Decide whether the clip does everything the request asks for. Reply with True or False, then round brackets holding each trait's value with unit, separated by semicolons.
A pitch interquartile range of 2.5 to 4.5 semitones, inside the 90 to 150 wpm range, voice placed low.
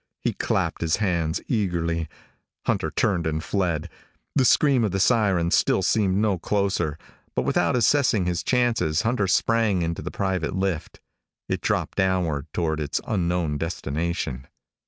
True (4.1 semitones; 145 wpm; 90 Hz)